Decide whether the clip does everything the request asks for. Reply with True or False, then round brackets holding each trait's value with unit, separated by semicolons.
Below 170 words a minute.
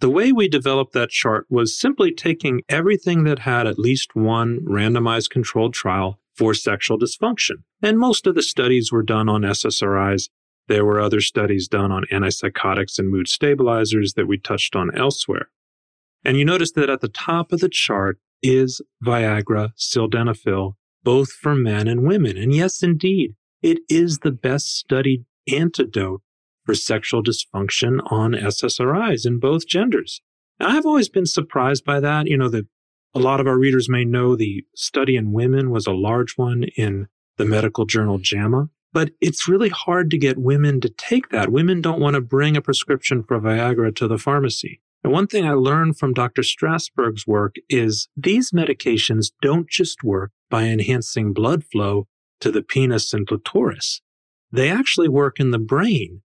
False (175 wpm)